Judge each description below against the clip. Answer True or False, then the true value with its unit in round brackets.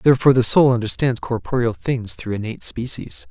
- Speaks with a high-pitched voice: False (120 Hz)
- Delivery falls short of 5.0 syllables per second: False (5.9 syllables/s)